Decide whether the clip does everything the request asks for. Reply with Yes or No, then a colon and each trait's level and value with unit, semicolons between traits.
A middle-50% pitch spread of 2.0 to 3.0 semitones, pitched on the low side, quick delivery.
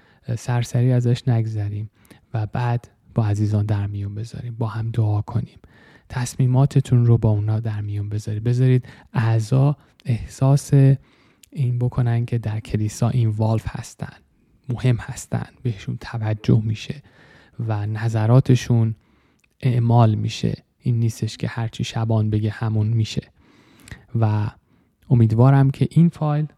No: narrow, 2.6 semitones; low, 115 Hz; average, 125 wpm